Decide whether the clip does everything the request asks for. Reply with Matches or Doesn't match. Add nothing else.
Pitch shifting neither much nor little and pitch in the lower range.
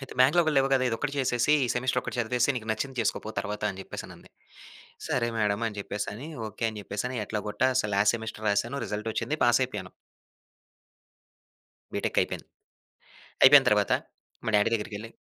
Matches